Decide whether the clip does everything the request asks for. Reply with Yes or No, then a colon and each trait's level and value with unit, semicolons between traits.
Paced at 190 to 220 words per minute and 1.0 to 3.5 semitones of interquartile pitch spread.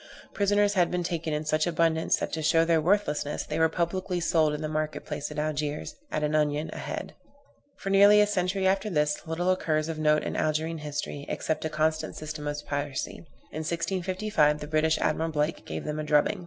Yes: fast, 205 wpm; average, 2.7 semitones